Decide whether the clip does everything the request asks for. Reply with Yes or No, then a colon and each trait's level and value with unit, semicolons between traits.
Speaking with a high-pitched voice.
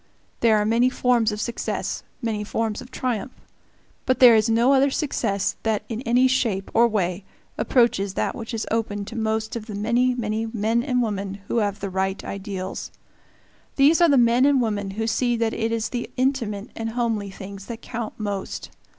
Yes: high, 225 Hz